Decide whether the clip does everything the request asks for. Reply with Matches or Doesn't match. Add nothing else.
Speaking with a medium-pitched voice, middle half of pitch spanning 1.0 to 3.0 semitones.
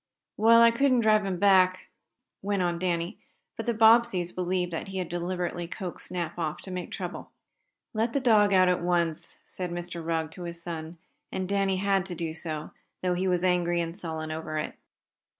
Matches